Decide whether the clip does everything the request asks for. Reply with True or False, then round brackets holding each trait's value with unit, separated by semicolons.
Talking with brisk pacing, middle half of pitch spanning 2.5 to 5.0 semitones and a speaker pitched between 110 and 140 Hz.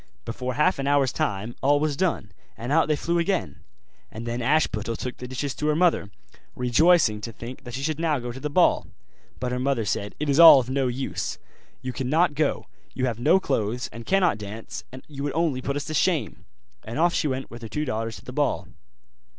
True (225 wpm; 4.3 semitones; 135 Hz)